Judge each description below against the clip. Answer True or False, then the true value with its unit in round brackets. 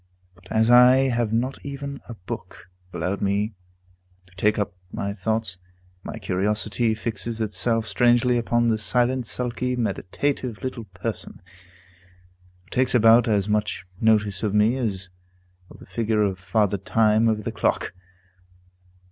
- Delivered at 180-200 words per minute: False (140 wpm)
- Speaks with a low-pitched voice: True (110 Hz)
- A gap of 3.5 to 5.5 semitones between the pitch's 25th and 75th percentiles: False (2.9 semitones)